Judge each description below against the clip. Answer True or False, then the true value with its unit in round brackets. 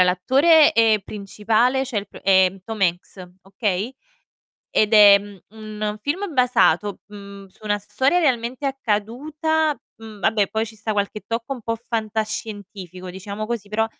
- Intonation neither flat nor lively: True (3.3 semitones)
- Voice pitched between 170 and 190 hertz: False (215 Hz)